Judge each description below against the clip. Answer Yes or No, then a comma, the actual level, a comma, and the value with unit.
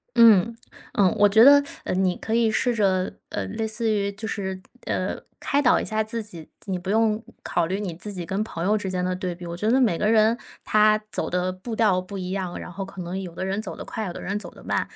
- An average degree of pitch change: Yes, average, 3.0 semitones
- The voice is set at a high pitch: Yes, high, 200 Hz